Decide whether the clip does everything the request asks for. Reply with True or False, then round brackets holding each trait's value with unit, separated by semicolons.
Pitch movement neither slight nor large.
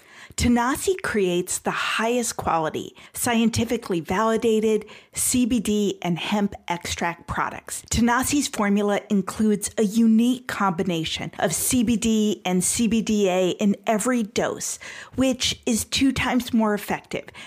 True (3.2 semitones)